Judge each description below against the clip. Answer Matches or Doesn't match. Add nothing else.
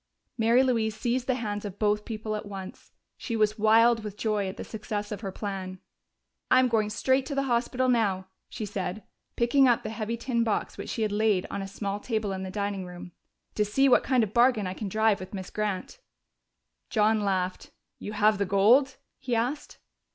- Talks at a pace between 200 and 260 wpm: Matches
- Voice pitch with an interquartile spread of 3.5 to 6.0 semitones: Doesn't match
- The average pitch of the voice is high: Matches